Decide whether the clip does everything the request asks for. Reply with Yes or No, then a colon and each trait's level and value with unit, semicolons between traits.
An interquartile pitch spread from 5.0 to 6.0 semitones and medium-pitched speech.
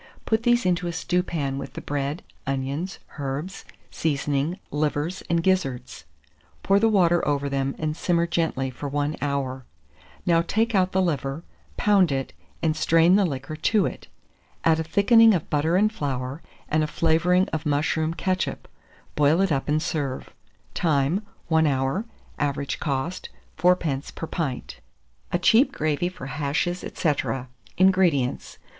No: average, 4.2 semitones; medium, 160 Hz